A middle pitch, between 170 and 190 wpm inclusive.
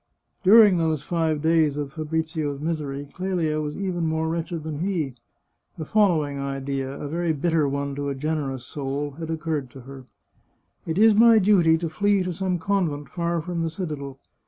Yes: medium, 160 Hz; average, 180 wpm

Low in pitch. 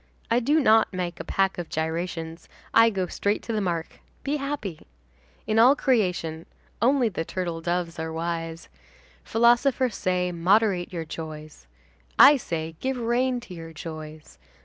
No: medium, 180 Hz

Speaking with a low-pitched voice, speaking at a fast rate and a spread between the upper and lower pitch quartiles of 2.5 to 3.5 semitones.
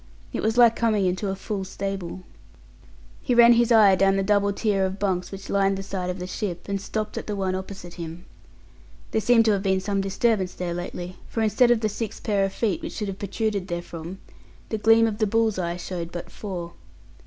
No: high, 195 Hz; fast, 220 wpm; average, 2.8 semitones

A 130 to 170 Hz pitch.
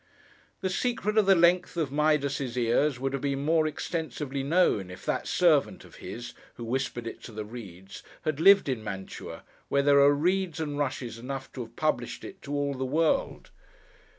Yes: medium, 140 Hz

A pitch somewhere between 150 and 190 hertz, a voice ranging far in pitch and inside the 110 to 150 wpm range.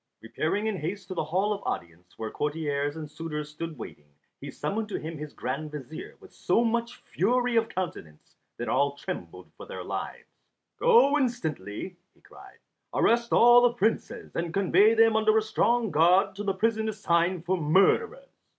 No: medium, 185 Hz; wide, 6.7 semitones; average, 175 wpm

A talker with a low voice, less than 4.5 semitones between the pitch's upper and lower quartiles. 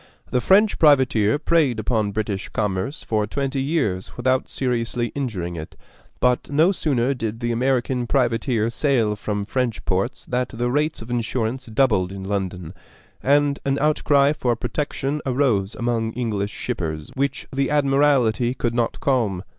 Yes: low, 120 Hz; average, 4.1 semitones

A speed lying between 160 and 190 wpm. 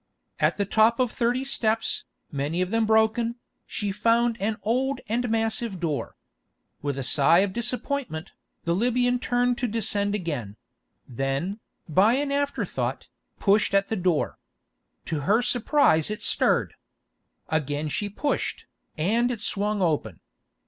No: average, 140 wpm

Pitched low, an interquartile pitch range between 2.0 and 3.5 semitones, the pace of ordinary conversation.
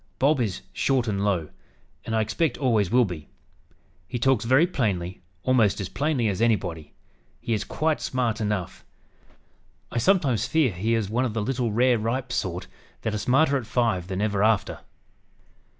No: low, 115 Hz; average, 4.0 semitones; average, 170 wpm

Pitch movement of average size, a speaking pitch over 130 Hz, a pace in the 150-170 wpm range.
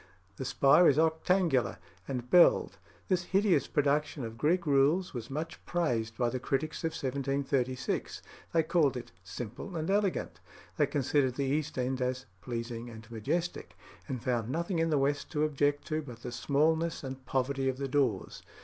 Yes: average, 4.1 semitones; medium, 140 Hz; average, 165 wpm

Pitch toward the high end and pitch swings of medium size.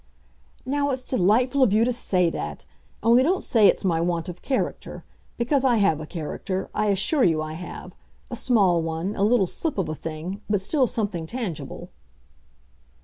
No: high, 200 Hz; wide, 6.4 semitones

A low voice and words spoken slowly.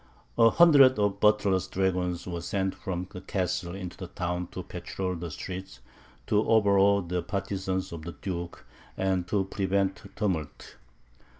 No: very low, 95 Hz; average, 145 wpm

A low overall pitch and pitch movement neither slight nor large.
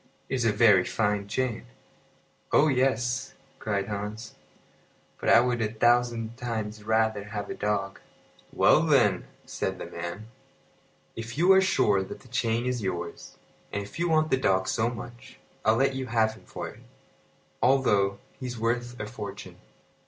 Yes: low, 115 Hz; average, 3.1 semitones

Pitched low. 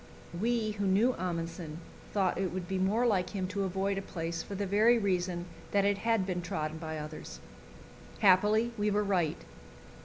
No: high, 190 Hz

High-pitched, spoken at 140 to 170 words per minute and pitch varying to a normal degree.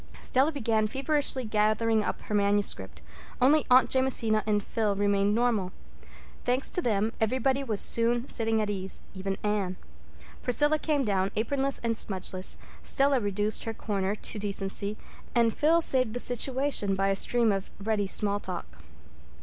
Yes: high, 220 Hz; average, 150 wpm; average, 4.1 semitones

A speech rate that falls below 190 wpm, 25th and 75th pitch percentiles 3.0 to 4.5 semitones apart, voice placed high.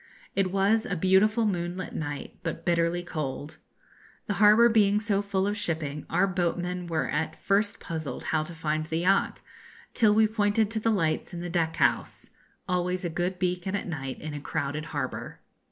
No: average, 180 wpm; average, 4.0 semitones; medium, 180 Hz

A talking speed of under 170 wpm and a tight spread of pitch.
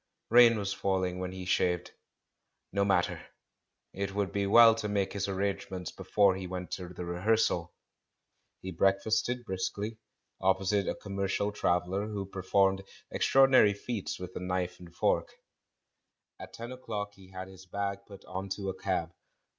Yes: average, 160 wpm; narrow, 1.8 semitones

